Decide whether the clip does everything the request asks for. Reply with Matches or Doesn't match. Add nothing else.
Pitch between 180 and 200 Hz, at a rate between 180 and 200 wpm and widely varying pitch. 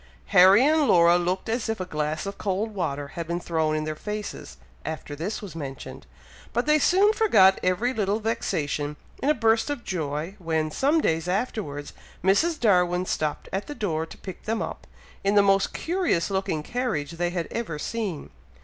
Matches